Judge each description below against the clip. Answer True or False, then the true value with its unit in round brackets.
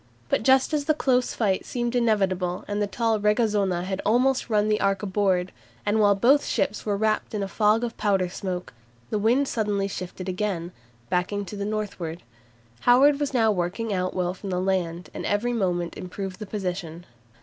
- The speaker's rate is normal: True (185 wpm)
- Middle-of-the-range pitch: False (205 Hz)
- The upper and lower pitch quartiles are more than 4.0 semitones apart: False (3.4 semitones)